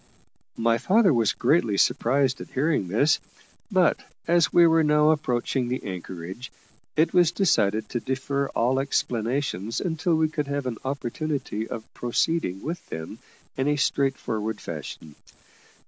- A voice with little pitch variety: No, average, 5.2 semitones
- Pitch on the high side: No, low, 135 Hz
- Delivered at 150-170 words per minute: No, average, 140 wpm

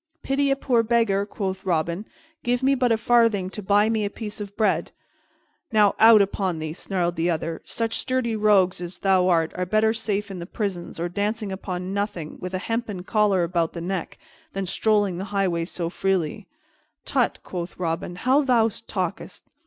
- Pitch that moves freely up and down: No, average, 3.6 semitones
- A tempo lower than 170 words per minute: No, average, 185 wpm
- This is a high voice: Yes, high, 195 Hz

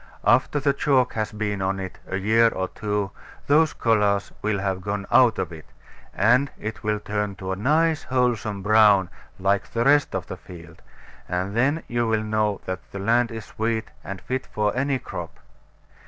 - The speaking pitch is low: Yes, low, 105 Hz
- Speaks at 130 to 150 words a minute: No, average, 185 wpm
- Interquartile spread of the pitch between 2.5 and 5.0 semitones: Yes, average, 3.7 semitones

